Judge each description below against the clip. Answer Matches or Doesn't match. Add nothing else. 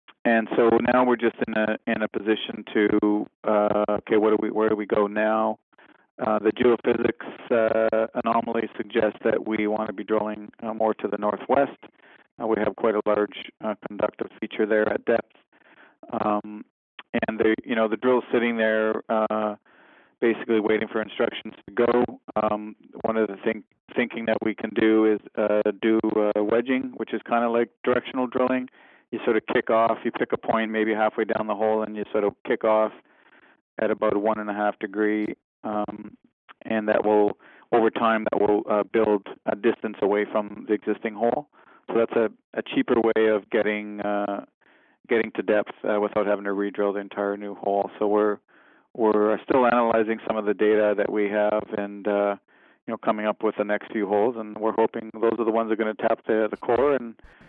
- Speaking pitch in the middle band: Doesn't match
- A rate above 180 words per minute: Matches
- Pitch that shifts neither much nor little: Doesn't match